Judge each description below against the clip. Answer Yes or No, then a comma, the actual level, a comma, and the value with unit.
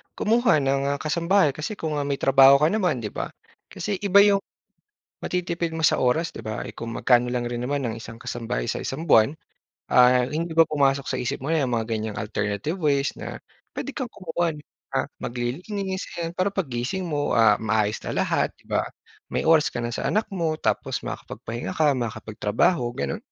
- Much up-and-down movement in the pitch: Yes, wide, 5.9 semitones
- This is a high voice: No, medium, 140 Hz